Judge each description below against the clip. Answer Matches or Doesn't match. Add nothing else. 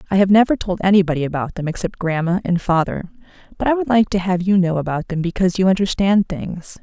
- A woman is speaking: Matches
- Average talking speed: Doesn't match